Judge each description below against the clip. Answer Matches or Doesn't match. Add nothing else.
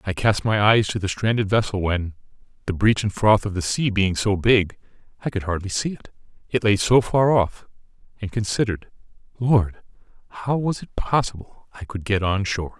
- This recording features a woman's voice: Doesn't match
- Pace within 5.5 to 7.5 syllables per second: Doesn't match